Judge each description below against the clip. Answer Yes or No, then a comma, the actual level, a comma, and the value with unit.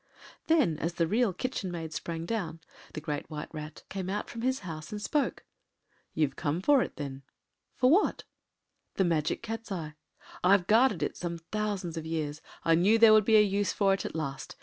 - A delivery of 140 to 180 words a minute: No, average, 195 wpm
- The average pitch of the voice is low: No, medium, 180 Hz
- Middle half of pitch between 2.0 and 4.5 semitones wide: No, average, 5.2 semitones